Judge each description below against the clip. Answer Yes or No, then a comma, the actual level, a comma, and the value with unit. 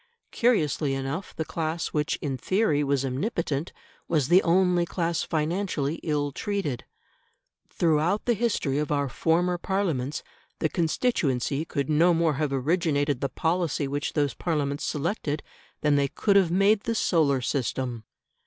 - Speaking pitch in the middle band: Yes, medium, 155 Hz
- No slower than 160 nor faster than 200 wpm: No, average, 145 wpm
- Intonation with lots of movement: No, average, 3.9 semitones